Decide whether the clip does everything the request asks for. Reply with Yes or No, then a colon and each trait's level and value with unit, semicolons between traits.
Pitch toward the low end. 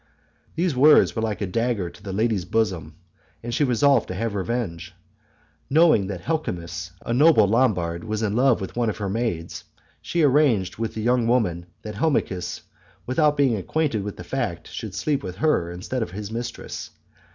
Yes: low, 110 Hz